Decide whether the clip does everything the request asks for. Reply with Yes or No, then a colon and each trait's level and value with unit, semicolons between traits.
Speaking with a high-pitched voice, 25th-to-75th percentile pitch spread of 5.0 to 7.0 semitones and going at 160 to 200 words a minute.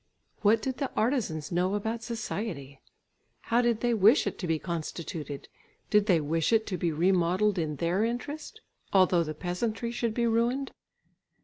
Yes: high, 205 Hz; wide, 5.6 semitones; average, 165 wpm